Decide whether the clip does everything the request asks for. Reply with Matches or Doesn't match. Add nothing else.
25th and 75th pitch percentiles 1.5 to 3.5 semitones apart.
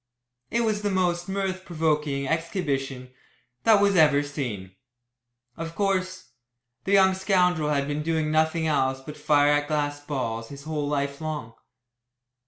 Doesn't match